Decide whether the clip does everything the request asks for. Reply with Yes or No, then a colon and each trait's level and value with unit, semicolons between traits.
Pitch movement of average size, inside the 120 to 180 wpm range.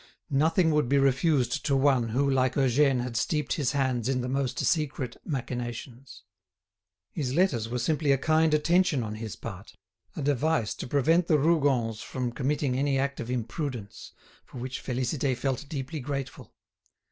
Yes: average, 3.2 semitones; average, 160 wpm